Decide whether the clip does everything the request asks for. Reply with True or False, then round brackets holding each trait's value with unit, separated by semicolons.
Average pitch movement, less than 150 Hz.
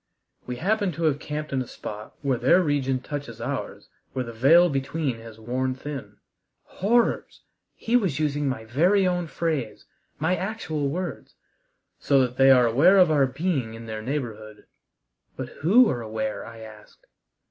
False (5.8 semitones; 140 Hz)